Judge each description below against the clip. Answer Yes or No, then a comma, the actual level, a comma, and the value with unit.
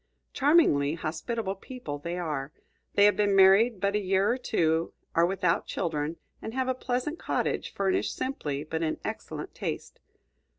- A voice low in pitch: No, high, 190 Hz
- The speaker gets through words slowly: No, average, 160 wpm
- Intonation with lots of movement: Yes, wide, 6.0 semitones